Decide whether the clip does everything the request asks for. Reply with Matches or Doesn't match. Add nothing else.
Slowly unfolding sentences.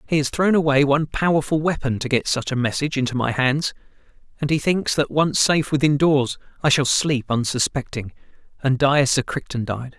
Doesn't match